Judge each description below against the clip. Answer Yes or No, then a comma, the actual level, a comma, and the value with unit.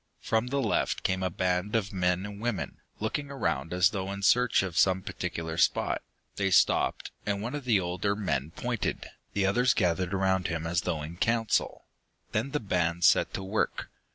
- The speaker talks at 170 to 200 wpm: Yes, average, 185 wpm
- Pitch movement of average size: Yes, average, 3.6 semitones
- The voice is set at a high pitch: No, very low, 95 Hz